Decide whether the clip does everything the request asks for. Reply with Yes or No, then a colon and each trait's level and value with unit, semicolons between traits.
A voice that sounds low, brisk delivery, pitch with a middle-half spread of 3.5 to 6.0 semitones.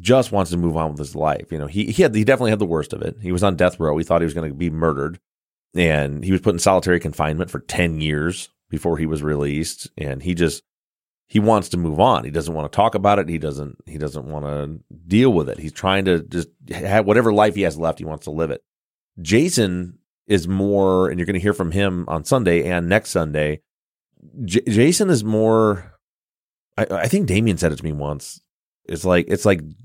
Yes: very low, 85 Hz; fast, 235 wpm; average, 4.2 semitones